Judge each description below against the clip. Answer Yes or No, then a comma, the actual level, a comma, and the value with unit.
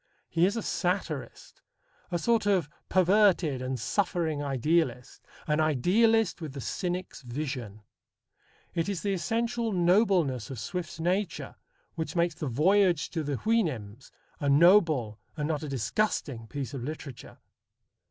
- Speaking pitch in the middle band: Yes, medium, 160 Hz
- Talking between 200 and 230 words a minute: No, slow, 135 wpm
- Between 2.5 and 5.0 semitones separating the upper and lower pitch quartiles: No, wide, 5.6 semitones